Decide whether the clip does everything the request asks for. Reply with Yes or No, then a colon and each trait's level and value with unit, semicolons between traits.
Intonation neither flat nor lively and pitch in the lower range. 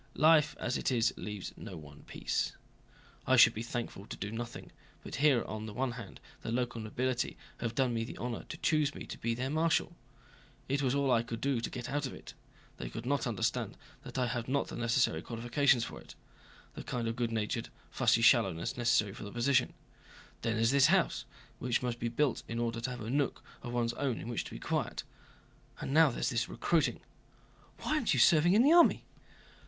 Yes: average, 3.1 semitones; low, 120 Hz